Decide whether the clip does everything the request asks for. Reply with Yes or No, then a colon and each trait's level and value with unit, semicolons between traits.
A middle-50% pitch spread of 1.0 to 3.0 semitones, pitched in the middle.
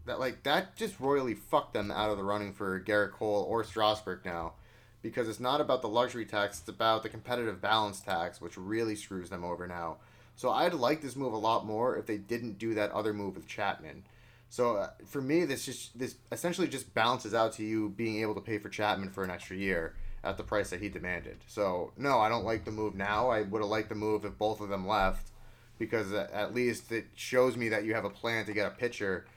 No: narrow, 2.6 semitones; low, 110 Hz